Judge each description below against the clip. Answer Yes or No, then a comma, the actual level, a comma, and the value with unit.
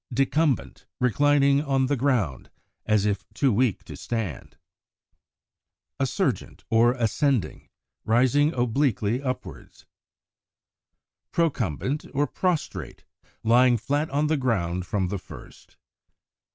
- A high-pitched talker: No, low, 125 Hz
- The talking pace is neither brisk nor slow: No, slow, 100 wpm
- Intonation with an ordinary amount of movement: Yes, average, 4.5 semitones